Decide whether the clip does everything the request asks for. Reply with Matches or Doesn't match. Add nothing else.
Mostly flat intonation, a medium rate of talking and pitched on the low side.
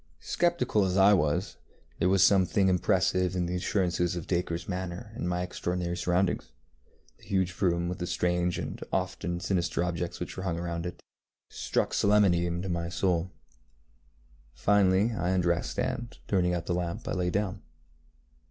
Matches